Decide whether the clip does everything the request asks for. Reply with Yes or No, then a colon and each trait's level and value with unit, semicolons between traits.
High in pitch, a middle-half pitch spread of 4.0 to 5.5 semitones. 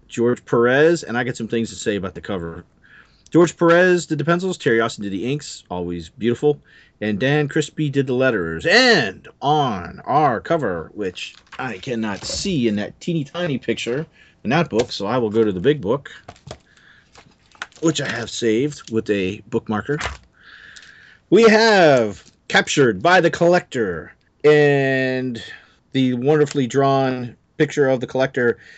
No: low, 130 Hz; average, 5.1 semitones